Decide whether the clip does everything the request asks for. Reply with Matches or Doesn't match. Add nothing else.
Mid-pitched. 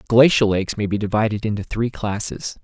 Doesn't match